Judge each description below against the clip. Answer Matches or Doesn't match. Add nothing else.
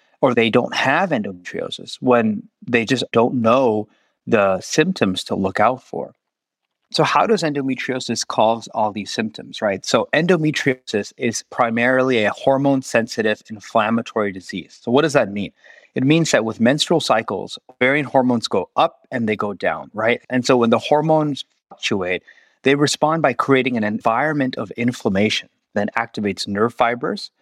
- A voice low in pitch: Matches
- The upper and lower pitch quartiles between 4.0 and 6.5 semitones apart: Matches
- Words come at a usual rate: Matches